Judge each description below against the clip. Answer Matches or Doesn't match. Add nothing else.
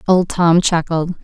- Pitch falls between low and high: Matches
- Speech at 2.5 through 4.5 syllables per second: Matches